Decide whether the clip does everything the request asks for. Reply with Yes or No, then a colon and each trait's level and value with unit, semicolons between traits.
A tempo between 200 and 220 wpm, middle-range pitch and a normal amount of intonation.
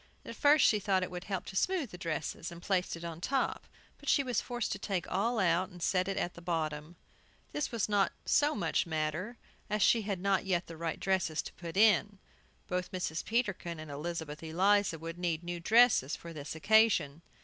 Yes: fast, 205 wpm; medium, 180 Hz; average, 3.8 semitones